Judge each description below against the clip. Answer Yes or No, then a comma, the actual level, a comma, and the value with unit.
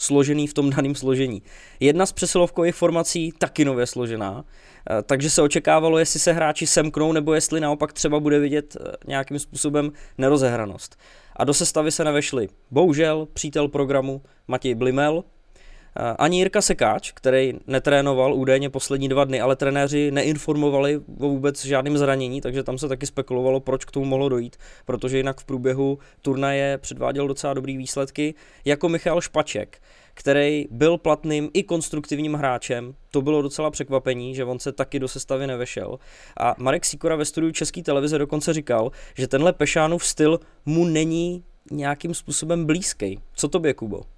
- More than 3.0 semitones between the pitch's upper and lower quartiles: No, narrow, 2.6 semitones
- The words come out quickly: No, average, 155 wpm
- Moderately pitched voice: Yes, medium, 145 Hz